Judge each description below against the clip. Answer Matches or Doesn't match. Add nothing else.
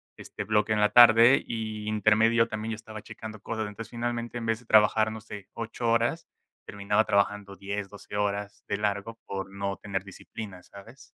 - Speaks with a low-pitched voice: Matches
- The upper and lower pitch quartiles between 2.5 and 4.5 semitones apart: Doesn't match